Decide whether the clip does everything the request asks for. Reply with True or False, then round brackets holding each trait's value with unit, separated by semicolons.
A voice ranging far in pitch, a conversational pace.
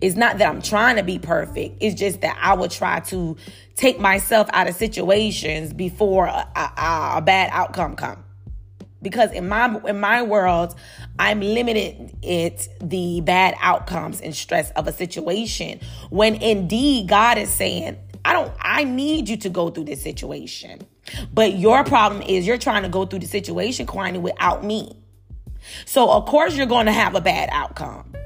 False (4.1 semitones; 175 wpm)